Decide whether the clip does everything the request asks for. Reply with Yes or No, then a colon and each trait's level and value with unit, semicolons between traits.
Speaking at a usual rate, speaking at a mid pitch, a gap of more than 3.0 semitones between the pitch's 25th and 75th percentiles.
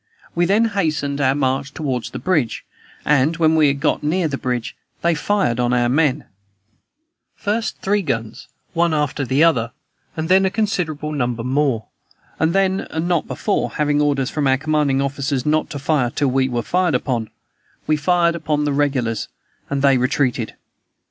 Yes: average, 175 wpm; medium, 145 Hz; average, 3.8 semitones